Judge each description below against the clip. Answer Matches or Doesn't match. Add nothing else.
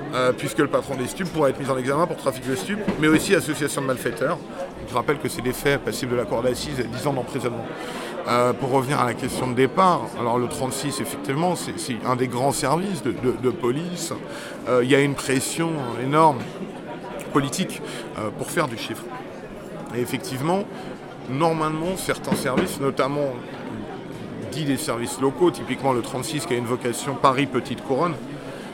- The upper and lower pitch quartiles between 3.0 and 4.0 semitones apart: Matches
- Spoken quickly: Doesn't match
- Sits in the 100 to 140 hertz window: Matches